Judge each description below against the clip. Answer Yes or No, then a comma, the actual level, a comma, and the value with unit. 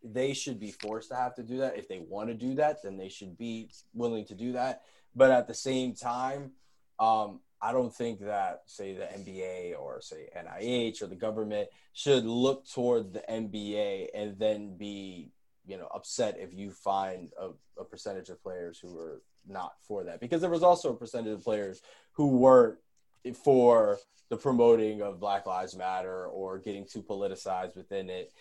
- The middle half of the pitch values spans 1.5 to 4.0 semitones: No, average, 4.7 semitones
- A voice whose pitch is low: Yes, low, 115 Hz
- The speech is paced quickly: No, average, 190 wpm